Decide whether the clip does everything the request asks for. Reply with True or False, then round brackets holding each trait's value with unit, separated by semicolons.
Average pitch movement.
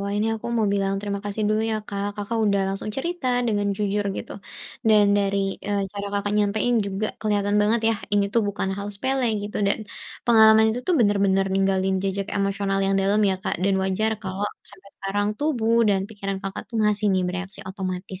False (1.6 semitones)